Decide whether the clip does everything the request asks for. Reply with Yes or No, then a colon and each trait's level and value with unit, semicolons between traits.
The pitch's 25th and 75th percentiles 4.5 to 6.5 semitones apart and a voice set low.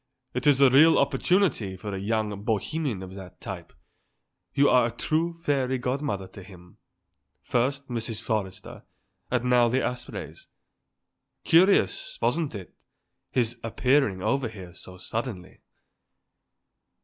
Yes: wide, 5.5 semitones; low, 120 Hz